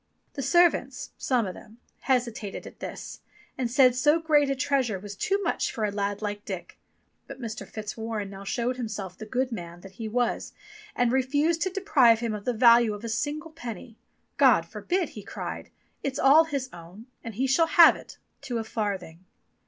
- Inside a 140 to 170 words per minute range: No, average, 190 wpm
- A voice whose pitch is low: No, high, 235 Hz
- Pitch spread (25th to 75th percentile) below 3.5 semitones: No, average, 4.6 semitones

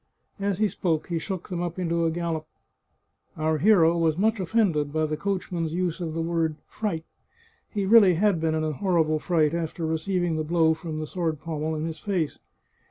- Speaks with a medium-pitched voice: Yes, medium, 165 Hz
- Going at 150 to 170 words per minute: No, average, 195 wpm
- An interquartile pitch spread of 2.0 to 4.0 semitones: Yes, narrow, 2.5 semitones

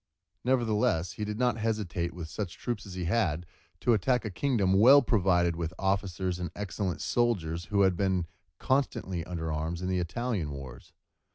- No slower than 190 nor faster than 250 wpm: No, average, 170 wpm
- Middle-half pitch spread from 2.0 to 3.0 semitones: No, average, 4.5 semitones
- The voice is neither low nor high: No, very low, 95 Hz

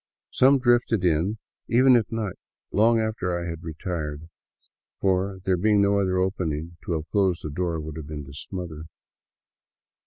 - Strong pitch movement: No, average, 4.5 semitones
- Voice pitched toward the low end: Yes, very low, 90 Hz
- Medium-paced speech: Yes, average, 160 wpm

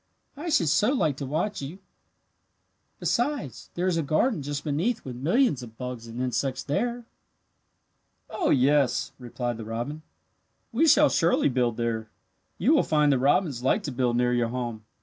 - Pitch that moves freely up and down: Yes, wide, 7.3 semitones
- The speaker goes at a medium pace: Yes, average, 170 wpm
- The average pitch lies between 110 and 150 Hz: Yes, medium, 140 Hz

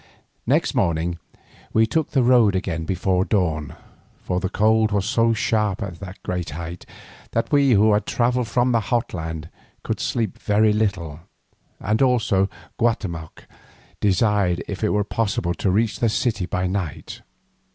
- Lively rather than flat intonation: No, average, 3.8 semitones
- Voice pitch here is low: Yes, low, 100 Hz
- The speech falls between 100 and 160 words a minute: Yes, average, 155 wpm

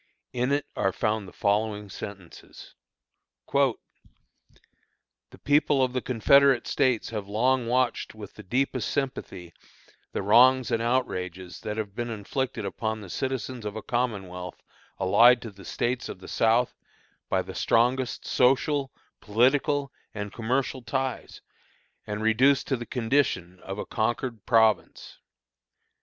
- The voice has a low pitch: Yes, low, 115 Hz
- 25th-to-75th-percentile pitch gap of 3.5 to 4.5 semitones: Yes, average, 4.0 semitones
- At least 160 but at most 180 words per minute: No, slow, 135 wpm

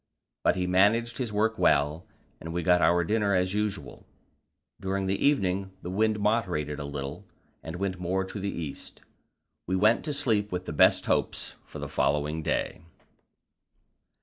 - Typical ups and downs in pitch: Yes, average, 3.6 semitones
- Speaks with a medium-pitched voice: No, very low, 95 Hz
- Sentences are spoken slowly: No, average, 165 wpm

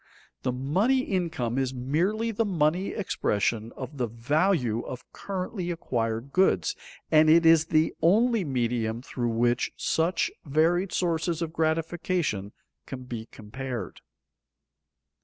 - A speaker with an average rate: No, slow, 120 wpm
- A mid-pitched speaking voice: Yes, medium, 155 Hz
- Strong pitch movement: Yes, wide, 6.3 semitones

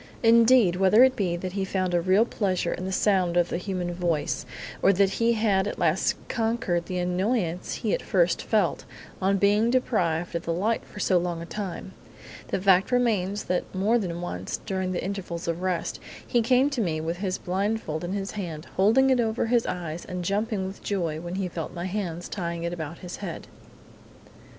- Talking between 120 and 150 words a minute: No, average, 200 wpm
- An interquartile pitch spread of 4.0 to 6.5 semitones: No, average, 3.3 semitones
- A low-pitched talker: No, medium, 185 Hz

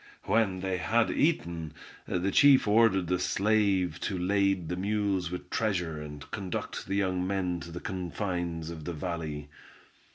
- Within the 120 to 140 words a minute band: No, average, 155 wpm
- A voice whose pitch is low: Yes, very low, 90 Hz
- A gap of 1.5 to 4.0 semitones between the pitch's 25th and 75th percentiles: Yes, average, 2.7 semitones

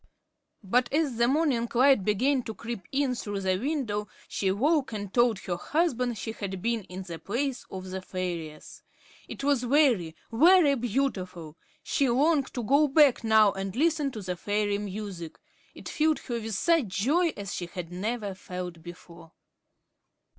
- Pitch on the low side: No, high, 225 Hz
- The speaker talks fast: No, average, 165 wpm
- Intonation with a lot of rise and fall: Yes, wide, 6.4 semitones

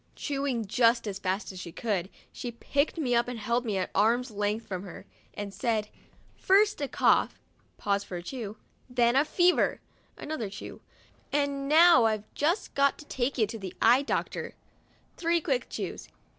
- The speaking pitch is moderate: No, high, 235 Hz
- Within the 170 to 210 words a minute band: Yes, average, 175 wpm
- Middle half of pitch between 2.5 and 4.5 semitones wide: No, wide, 5.4 semitones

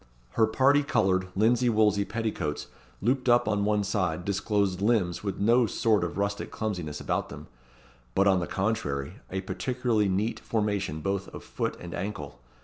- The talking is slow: No, average, 160 wpm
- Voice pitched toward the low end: Yes, low, 100 Hz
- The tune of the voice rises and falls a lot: No, average, 3.2 semitones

